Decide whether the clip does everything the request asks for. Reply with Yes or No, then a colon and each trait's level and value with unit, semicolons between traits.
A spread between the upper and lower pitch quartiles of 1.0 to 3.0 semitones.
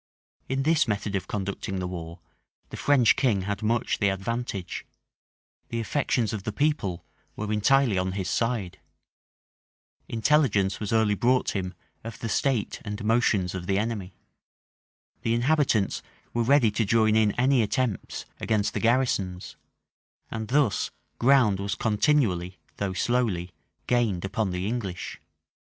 No: average, 3.8 semitones